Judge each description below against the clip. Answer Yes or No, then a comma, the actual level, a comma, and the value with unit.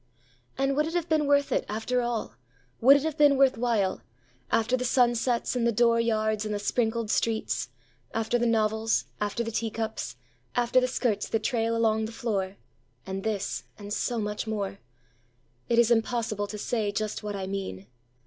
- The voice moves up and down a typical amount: Yes, average, 3.1 semitones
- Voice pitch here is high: Yes, high, 220 Hz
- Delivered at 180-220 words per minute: No, average, 160 wpm